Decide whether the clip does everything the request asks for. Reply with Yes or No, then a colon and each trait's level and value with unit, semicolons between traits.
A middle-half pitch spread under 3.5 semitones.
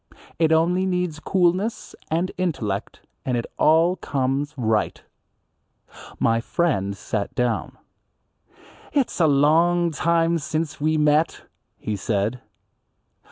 No: wide, 5.6 semitones